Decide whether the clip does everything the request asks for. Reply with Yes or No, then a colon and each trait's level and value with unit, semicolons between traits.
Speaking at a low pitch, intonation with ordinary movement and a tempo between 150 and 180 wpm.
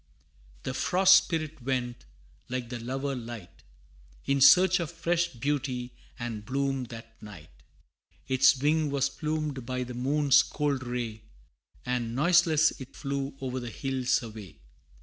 No: low, 130 Hz; average, 3.4 semitones; slow, 135 wpm